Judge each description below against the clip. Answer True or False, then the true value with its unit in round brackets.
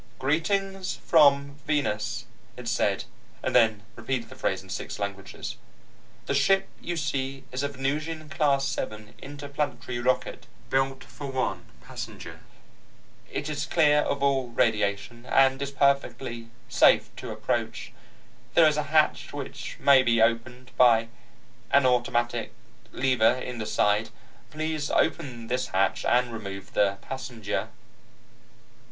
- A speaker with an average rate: False (130 wpm)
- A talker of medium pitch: False (130 Hz)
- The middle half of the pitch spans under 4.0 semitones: True (3.6 semitones)